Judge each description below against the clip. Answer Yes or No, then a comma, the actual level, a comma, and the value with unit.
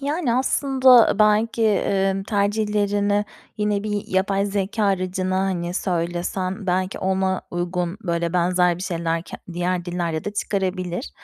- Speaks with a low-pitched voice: No, high, 190 Hz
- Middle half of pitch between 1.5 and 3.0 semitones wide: Yes, average, 2.7 semitones